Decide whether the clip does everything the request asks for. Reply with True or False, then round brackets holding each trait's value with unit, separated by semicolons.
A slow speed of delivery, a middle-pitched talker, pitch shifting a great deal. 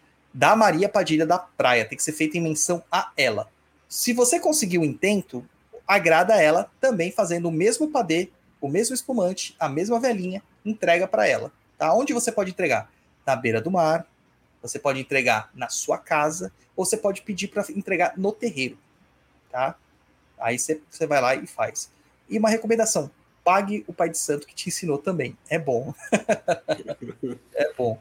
False (175 wpm; 175 Hz; 5.8 semitones)